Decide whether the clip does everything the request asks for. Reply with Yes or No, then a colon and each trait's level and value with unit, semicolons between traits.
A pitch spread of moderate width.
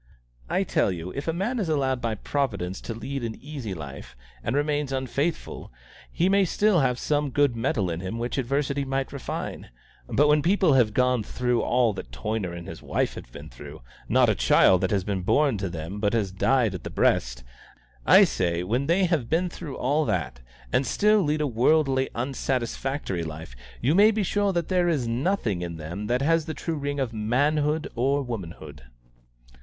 No: wide, 7.0 semitones